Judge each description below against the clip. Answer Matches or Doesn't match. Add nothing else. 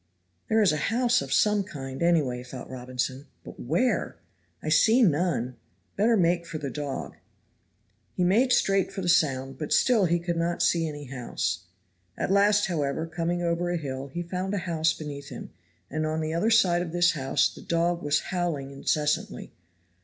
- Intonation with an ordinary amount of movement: Matches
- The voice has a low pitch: Doesn't match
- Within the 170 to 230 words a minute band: Matches